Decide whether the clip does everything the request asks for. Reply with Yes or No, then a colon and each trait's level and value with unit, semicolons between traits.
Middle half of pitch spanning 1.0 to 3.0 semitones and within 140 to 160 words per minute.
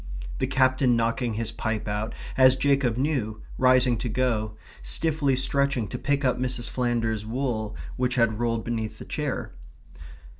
Yes: average, 2.7 semitones; average, 150 wpm